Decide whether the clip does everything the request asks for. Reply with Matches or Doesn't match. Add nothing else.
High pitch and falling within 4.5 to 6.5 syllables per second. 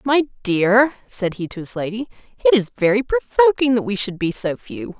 Matches